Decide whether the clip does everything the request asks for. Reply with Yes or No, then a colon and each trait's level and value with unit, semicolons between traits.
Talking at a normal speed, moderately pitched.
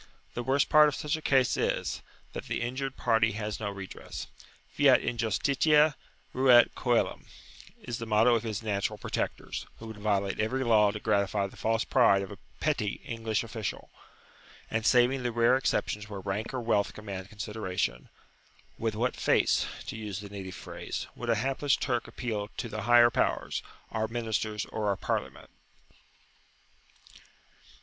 No: average, 160 wpm; low, 110 Hz